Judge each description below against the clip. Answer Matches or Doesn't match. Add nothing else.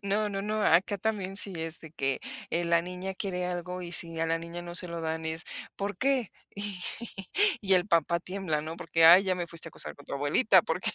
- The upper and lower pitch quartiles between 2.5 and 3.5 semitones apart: Matches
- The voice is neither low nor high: Matches